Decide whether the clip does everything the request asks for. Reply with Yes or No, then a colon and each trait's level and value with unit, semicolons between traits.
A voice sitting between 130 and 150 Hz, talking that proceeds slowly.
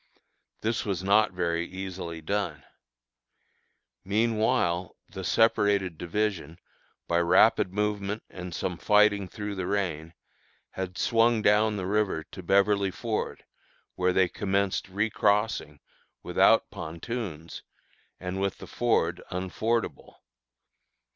No: very low, 95 Hz; slow, 110 wpm